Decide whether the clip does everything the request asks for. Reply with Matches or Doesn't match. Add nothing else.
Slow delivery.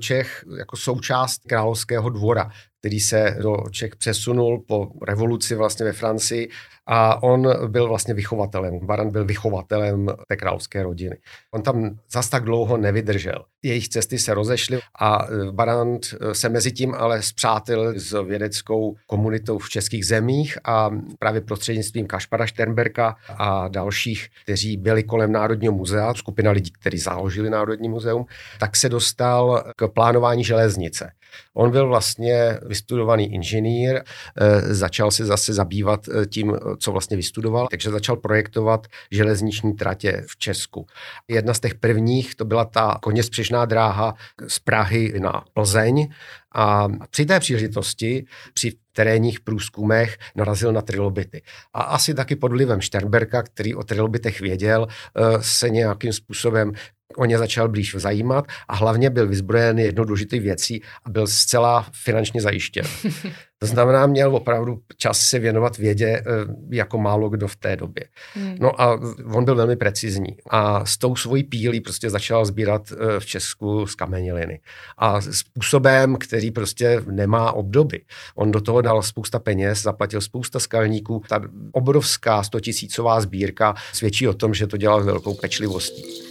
Doesn't match